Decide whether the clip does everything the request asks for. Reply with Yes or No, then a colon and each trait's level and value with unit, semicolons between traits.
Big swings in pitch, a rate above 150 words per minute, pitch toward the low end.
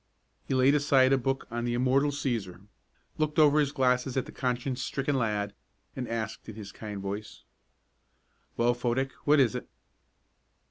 No: average, 2.9 semitones; average, 165 wpm; low, 125 Hz